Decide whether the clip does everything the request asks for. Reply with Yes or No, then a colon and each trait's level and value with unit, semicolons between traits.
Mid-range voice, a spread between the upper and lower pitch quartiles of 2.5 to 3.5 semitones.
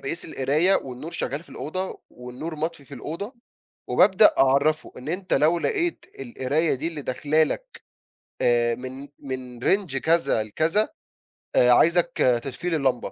No: medium, 150 Hz; average, 4.7 semitones